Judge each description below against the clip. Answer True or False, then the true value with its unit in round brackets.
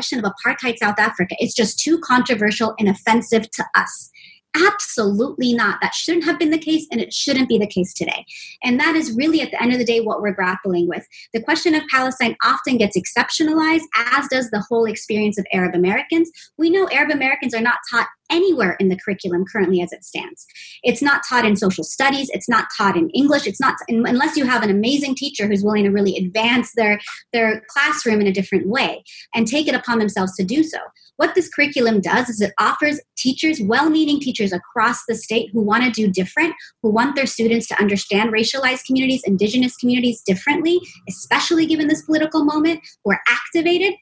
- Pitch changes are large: True (6.0 semitones)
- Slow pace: False (200 wpm)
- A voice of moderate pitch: False (240 Hz)